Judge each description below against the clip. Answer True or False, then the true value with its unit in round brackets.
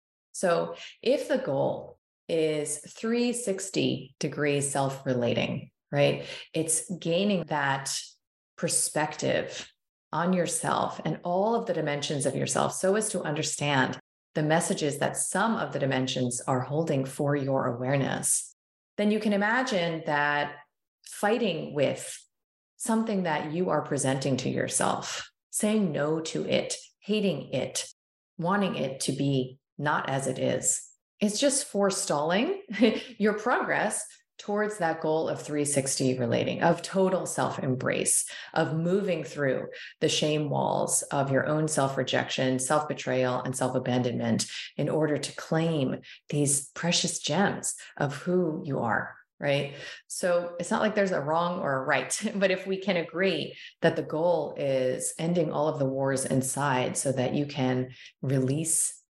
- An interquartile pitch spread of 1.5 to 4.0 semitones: False (5.0 semitones)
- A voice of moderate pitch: True (155 Hz)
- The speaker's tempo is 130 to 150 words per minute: True (140 wpm)